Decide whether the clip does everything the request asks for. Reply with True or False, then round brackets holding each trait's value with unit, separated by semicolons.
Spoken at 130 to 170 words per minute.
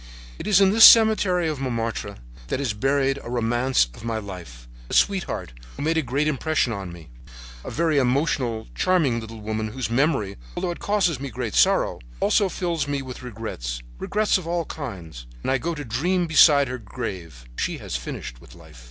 False (185 wpm)